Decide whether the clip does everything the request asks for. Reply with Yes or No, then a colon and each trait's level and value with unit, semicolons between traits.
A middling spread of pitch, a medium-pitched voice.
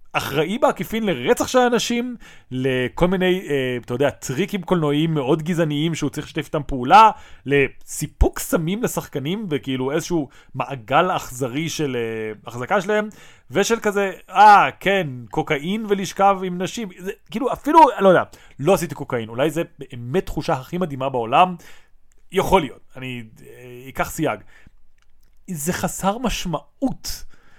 No: wide, 6.3 semitones; medium, 160 Hz